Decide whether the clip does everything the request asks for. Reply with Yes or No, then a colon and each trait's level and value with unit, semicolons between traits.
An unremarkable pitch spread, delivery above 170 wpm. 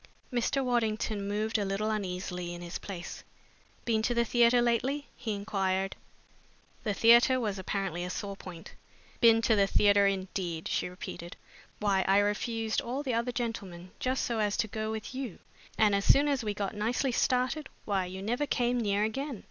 Yes: average, 3.5 semitones; average, 180 wpm